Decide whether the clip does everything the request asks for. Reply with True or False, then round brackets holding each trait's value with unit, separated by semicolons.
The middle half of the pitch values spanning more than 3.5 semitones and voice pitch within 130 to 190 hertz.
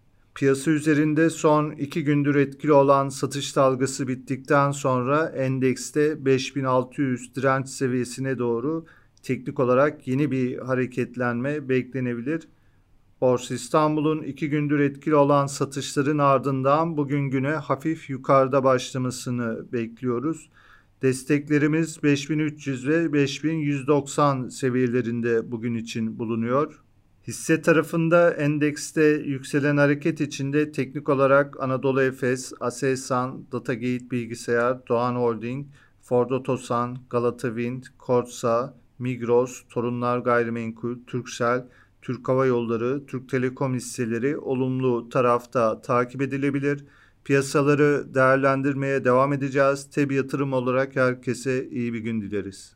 False (2.7 semitones; 135 Hz)